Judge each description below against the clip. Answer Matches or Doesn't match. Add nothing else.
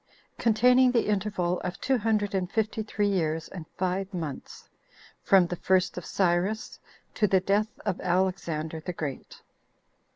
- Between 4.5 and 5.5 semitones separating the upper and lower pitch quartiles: Doesn't match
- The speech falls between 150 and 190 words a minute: Doesn't match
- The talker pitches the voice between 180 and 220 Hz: Matches